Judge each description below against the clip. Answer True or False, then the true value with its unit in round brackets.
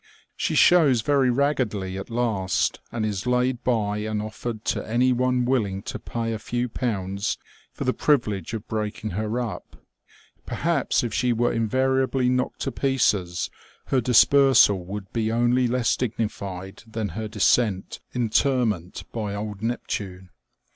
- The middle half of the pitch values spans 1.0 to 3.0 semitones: False (3.4 semitones)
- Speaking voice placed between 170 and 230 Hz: False (115 Hz)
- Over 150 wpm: False (145 wpm)